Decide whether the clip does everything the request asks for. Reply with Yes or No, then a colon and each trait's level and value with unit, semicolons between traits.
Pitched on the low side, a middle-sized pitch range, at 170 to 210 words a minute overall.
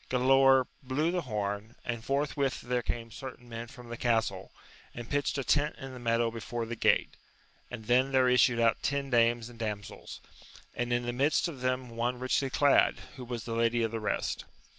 No: low, 120 Hz; narrow, 2.3 semitones; average, 195 wpm